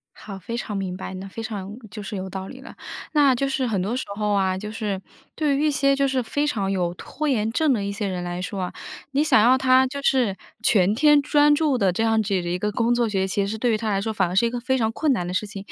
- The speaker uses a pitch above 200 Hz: Yes, high, 220 Hz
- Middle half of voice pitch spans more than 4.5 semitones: Yes, average, 5.2 semitones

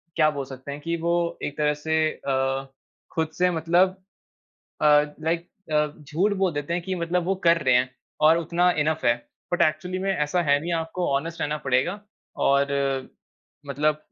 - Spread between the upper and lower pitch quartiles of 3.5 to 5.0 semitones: No, average, 3.1 semitones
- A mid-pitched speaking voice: Yes, medium, 160 Hz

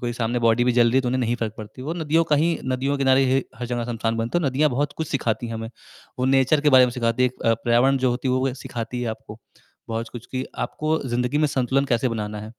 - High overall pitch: No, low, 125 Hz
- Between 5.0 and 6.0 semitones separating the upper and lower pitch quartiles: No, average, 2.7 semitones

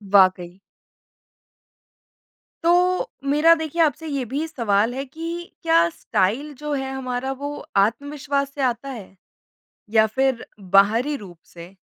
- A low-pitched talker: No, very high, 265 Hz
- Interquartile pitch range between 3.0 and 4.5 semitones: No, wide, 5.6 semitones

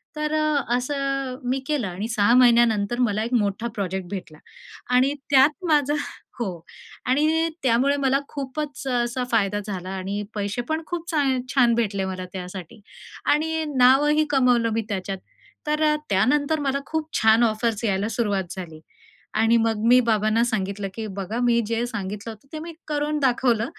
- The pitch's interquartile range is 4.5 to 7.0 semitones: Yes, average, 5.3 semitones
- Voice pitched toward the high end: Yes, high, 235 Hz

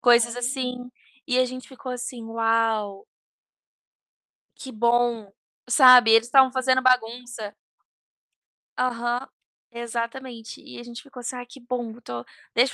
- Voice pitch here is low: No, high, 245 Hz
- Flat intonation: Yes, narrow, 1.7 semitones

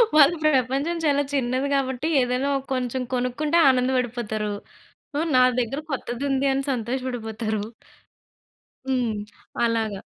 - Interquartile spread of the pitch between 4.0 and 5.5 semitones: No, narrow, 2.4 semitones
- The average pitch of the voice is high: Yes, very high, 255 Hz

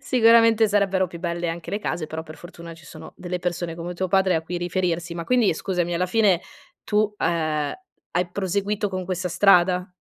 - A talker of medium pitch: Yes, medium, 180 Hz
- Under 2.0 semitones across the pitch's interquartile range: No, narrow, 2.6 semitones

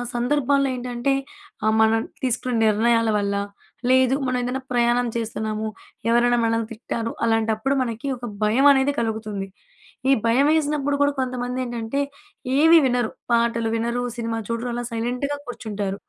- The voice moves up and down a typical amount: No, narrow, 2.2 semitones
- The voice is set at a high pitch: Yes, high, 240 Hz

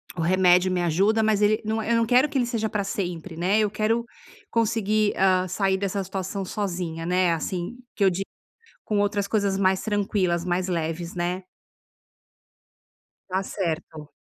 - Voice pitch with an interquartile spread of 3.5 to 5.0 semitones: No, average, 3.0 semitones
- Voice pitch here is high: Yes, high, 195 Hz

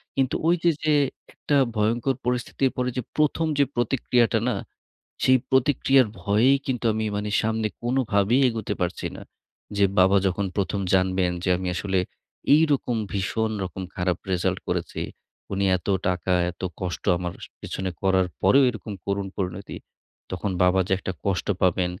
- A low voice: Yes, low, 105 Hz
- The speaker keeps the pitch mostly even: No, average, 4.8 semitones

